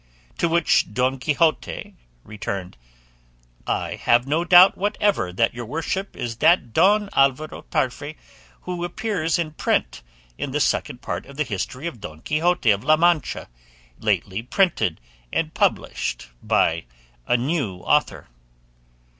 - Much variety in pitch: Yes, wide, 6.6 semitones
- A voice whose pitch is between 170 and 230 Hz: No, medium, 150 Hz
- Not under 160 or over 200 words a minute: No, slow, 135 wpm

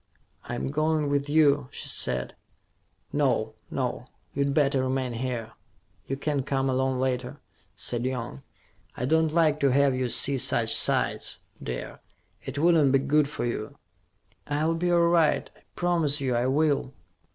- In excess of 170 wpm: No, average, 150 wpm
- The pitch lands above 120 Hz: Yes, medium, 140 Hz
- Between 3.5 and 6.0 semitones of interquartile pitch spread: No, average, 2.9 semitones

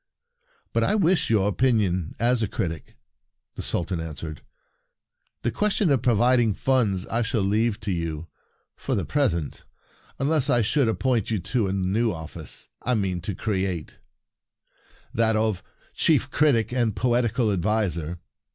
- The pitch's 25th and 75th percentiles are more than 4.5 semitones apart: Yes, average, 5.0 semitones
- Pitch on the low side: Yes, low, 110 Hz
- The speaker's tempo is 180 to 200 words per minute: No, average, 150 wpm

